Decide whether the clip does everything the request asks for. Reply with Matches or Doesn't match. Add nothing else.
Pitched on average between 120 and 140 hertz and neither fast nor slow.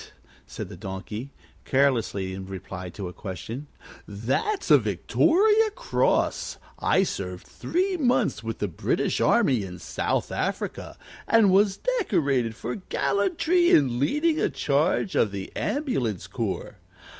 Doesn't match